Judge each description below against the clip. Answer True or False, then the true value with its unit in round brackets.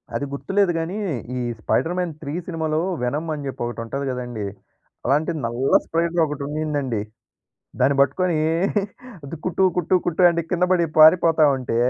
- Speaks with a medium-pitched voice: True (155 Hz)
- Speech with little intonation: False (3.8 semitones)